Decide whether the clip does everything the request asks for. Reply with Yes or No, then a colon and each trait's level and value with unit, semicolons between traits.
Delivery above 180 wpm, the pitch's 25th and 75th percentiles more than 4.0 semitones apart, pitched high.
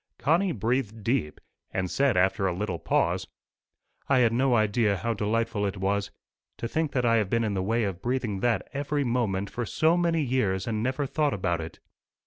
No: average, 195 wpm; average, 4.8 semitones; low, 115 Hz